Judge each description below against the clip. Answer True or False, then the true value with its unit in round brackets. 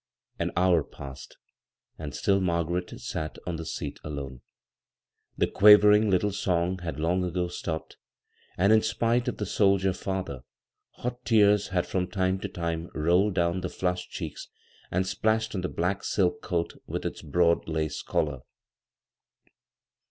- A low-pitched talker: True (90 Hz)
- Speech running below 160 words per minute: True (150 wpm)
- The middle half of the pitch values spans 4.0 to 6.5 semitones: False (3.1 semitones)